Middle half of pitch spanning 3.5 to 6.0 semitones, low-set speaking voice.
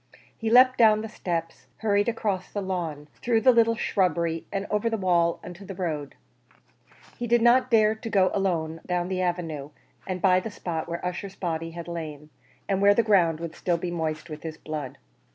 No: average, 4.3 semitones; medium, 180 Hz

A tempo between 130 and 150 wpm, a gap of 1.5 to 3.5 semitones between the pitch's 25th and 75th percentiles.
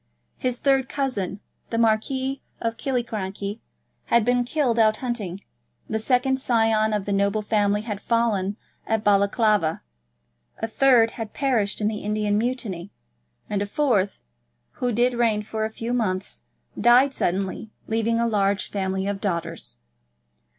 Yes: average, 145 wpm; average, 3.0 semitones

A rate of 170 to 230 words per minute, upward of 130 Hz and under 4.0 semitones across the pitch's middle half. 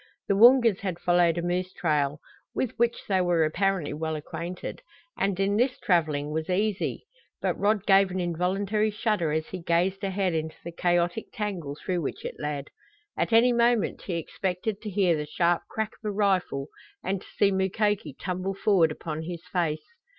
Yes: average, 180 wpm; medium, 185 Hz; average, 3.4 semitones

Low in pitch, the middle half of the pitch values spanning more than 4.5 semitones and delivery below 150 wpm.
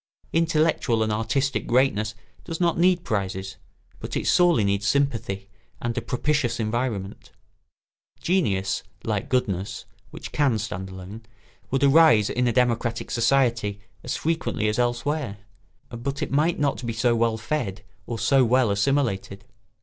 Yes: low, 120 Hz; average, 4.9 semitones; average, 140 wpm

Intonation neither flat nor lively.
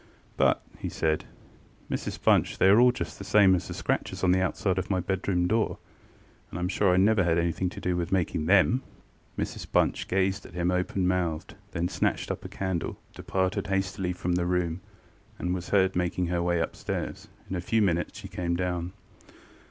No: narrow, 1.6 semitones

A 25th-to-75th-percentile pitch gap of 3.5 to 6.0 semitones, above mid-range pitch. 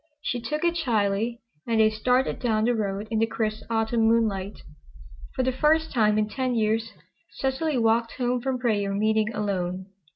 No: narrow, 2.6 semitones; high, 225 Hz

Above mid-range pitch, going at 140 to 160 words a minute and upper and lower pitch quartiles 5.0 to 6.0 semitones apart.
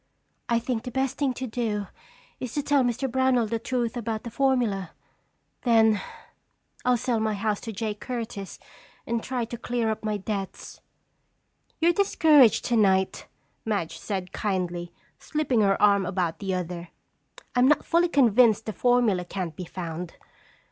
No: high, 225 Hz; average, 155 wpm; average, 4.1 semitones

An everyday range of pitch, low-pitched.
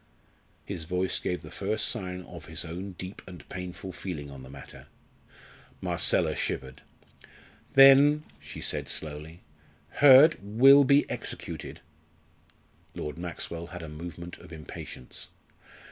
Yes: average, 4.5 semitones; very low, 90 Hz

